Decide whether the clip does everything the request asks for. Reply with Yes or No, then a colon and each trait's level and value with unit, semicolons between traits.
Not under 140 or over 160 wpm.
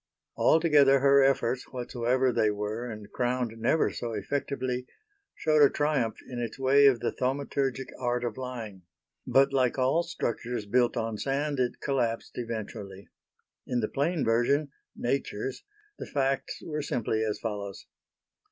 Yes: average, 145 wpm